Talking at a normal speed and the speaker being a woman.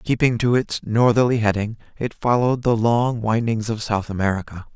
No: average, 165 wpm; male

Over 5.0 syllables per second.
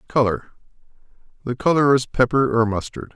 Yes: 5.4 syllables/s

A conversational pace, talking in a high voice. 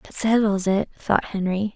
Yes: average, 170 wpm; high, 200 Hz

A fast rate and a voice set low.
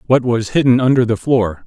Yes: fast, 215 wpm; low, 120 Hz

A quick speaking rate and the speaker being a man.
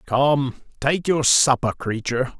No: slow, 125 wpm; male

